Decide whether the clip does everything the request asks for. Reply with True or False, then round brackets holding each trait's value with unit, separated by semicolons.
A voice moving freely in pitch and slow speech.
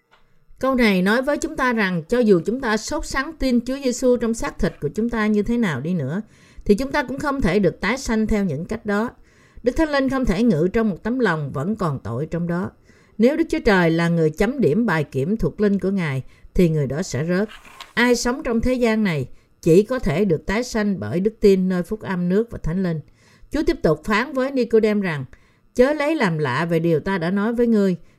False (5.9 semitones; 245 wpm)